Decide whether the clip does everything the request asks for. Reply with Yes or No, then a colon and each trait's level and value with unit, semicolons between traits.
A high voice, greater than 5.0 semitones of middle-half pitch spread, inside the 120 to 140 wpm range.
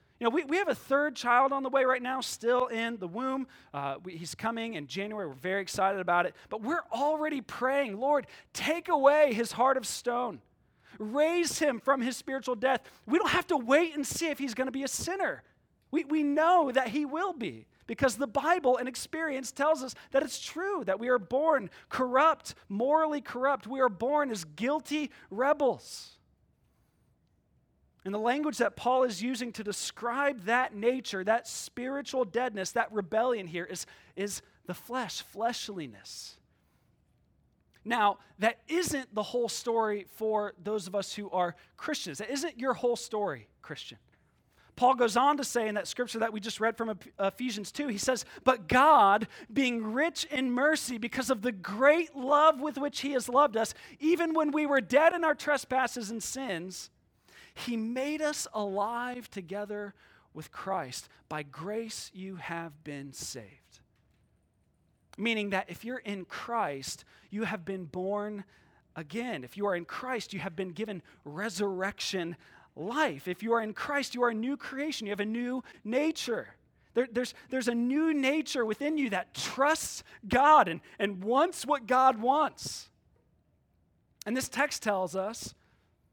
No: high, 245 Hz; wide, 5.4 semitones; average, 170 wpm